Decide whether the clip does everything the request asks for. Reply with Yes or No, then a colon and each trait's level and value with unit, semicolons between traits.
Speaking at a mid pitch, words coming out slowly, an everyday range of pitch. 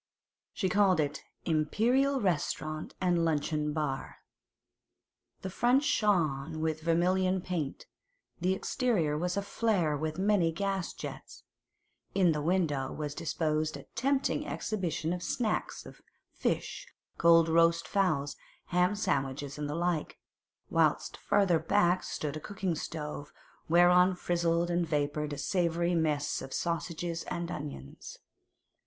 Yes: medium, 170 Hz; slow, 125 wpm; average, 3.5 semitones